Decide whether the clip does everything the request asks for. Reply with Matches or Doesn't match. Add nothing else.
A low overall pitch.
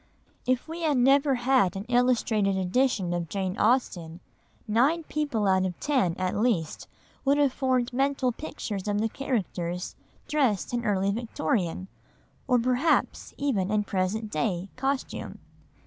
Doesn't match